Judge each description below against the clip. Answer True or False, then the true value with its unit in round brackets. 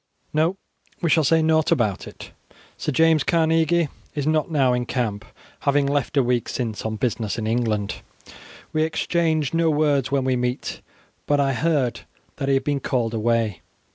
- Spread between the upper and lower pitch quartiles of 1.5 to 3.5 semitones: False (4.8 semitones)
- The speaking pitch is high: False (140 Hz)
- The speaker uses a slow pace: False (170 wpm)